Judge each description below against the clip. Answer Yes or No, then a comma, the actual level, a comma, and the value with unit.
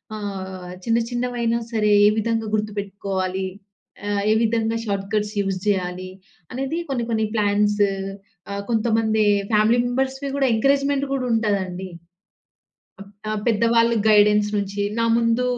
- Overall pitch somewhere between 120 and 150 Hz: No, high, 215 Hz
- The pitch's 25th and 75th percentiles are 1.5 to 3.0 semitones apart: Yes, narrow, 2.6 semitones